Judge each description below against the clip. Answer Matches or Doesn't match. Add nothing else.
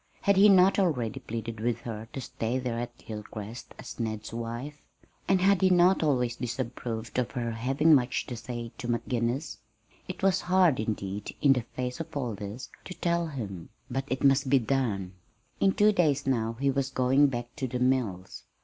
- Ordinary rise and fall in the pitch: Matches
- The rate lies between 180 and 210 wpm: Matches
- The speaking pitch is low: Matches